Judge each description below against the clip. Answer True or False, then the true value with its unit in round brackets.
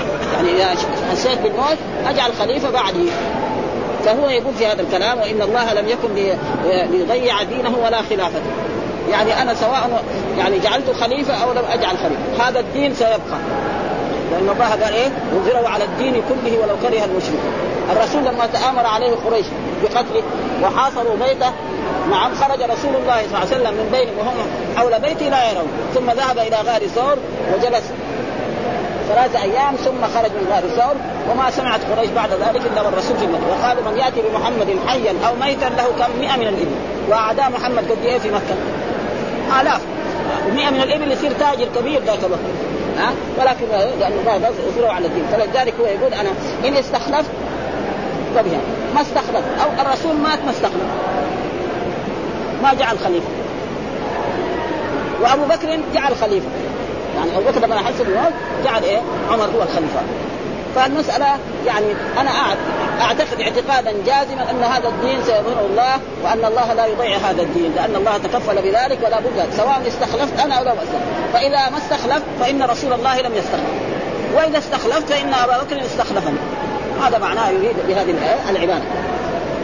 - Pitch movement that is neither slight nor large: True (3.4 semitones)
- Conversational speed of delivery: False (150 wpm)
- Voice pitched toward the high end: True (250 Hz)